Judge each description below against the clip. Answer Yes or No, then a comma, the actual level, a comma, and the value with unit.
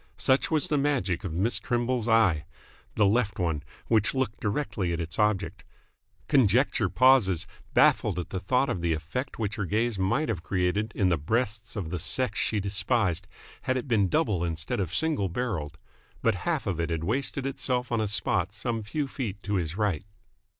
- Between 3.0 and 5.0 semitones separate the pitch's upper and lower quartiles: No, wide, 5.4 semitones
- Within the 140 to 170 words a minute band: No, average, 185 wpm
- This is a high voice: No, low, 105 Hz